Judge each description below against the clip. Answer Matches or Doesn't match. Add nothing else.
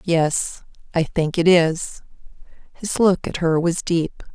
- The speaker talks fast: Doesn't match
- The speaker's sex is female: Matches